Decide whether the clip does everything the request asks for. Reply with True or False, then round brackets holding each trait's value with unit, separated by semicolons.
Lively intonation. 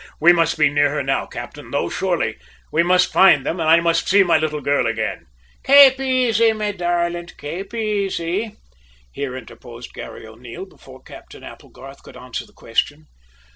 True (5.8 semitones)